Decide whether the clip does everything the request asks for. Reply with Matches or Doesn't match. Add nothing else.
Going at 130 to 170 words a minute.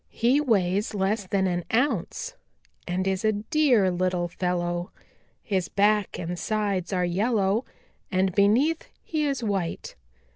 Matches